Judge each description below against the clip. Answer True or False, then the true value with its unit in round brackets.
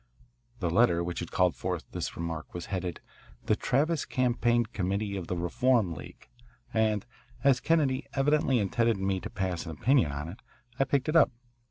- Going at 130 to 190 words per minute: True (175 wpm)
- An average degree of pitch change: False (6.7 semitones)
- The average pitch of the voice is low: True (105 Hz)